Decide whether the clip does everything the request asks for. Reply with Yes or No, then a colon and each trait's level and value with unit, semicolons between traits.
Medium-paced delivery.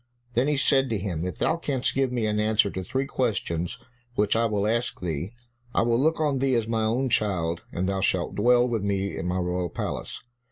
No: fast, 220 wpm